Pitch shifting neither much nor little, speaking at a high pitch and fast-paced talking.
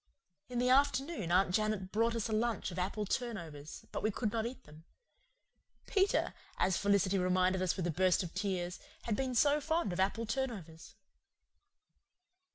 No: average, 4.6 semitones; high, 205 Hz; average, 165 wpm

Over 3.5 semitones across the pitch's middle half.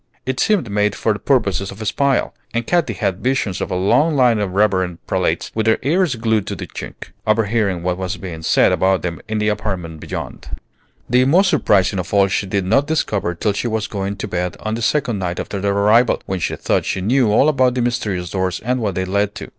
Yes: average, 4.3 semitones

